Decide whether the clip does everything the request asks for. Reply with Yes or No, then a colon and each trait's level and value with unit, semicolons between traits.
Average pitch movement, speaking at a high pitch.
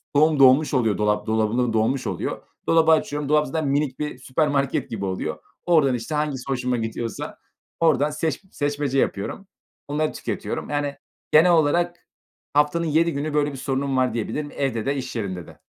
No: average, 3.3 semitones; medium, 140 Hz